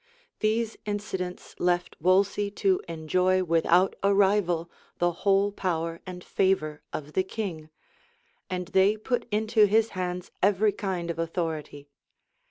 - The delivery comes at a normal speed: No, slow, 130 wpm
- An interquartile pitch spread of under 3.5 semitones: Yes, average, 3.1 semitones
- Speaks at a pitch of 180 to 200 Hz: Yes, medium, 185 Hz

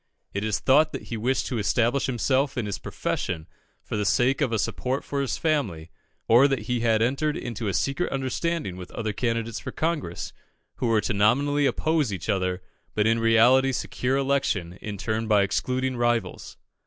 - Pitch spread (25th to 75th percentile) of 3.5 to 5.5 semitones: Yes, average, 4.4 semitones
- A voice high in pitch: No, low, 120 Hz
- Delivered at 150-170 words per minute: No, average, 185 wpm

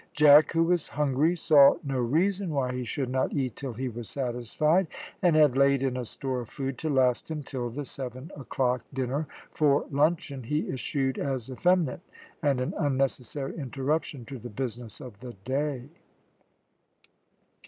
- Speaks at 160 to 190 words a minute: Yes, average, 165 wpm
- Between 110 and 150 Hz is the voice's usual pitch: Yes, low, 135 Hz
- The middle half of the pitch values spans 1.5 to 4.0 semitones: Yes, average, 2.9 semitones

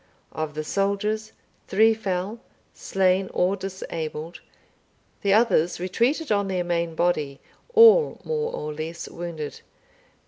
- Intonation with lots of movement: No, average, 4.3 semitones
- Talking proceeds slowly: Yes, slow, 115 wpm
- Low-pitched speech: No, medium, 185 Hz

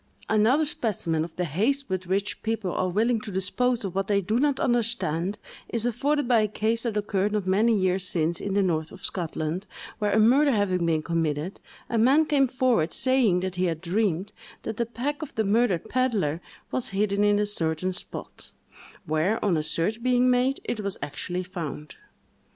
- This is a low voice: No, high, 205 Hz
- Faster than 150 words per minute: Yes, average, 190 wpm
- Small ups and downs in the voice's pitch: No, average, 4.7 semitones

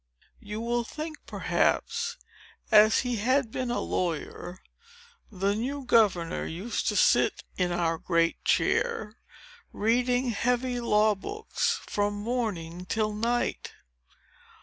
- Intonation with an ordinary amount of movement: Yes, average, 3.9 semitones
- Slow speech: Yes, slow, 120 wpm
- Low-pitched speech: No, high, 225 Hz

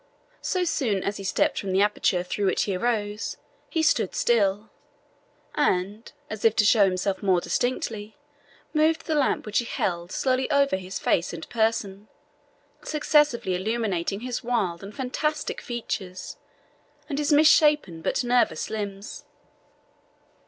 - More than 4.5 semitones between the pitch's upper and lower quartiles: Yes, average, 5.0 semitones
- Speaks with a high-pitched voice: Yes, high, 215 Hz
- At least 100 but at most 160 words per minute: Yes, average, 145 wpm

